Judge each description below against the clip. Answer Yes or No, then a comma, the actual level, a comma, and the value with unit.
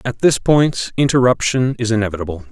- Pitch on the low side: Yes, low, 120 Hz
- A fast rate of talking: No, average, 145 wpm